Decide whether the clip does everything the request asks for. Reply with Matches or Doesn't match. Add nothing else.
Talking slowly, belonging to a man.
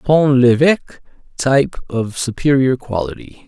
Matches